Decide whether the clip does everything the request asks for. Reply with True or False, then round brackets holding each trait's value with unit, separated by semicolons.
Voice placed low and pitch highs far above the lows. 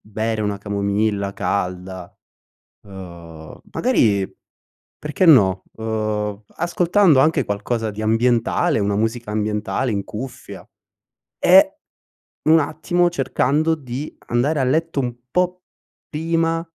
True (115 Hz; 7.2 semitones)